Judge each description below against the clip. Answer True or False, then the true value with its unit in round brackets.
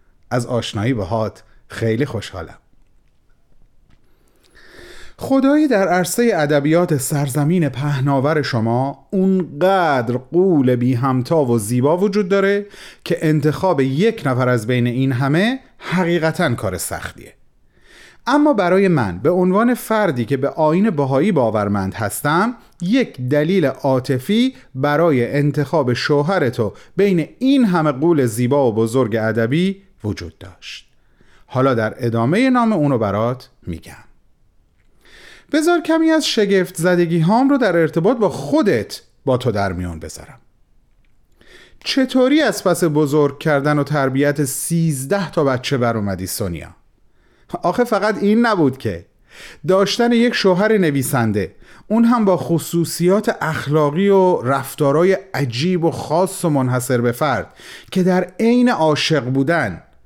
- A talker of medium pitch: True (150 Hz)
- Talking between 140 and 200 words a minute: False (125 wpm)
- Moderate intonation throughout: False (7.3 semitones)